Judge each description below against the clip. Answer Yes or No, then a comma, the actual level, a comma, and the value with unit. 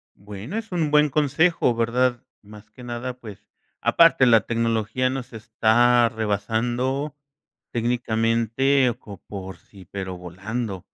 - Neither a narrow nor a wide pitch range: Yes, average, 3.1 semitones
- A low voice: Yes, low, 120 Hz